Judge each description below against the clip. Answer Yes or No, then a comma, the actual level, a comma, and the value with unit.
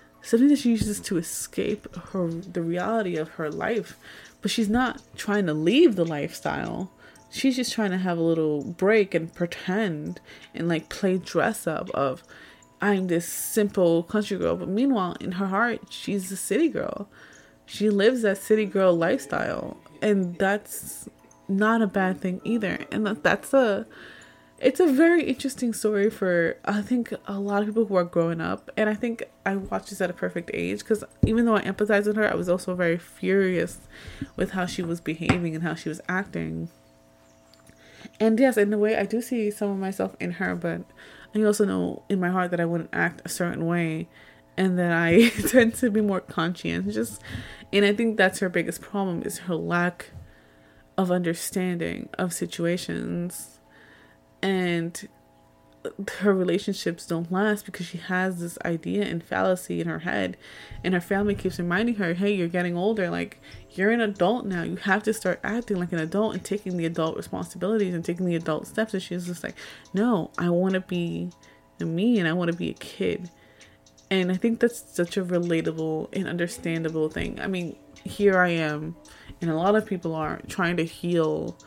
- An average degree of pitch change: Yes, average, 3.7 semitones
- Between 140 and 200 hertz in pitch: Yes, medium, 185 Hz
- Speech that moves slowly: No, average, 185 wpm